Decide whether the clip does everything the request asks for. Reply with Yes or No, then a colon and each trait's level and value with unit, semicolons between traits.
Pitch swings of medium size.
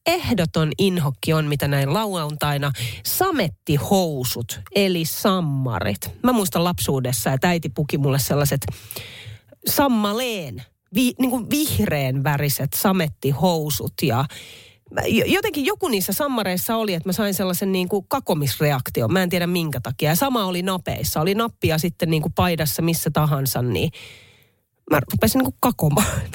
No: wide, 6.4 semitones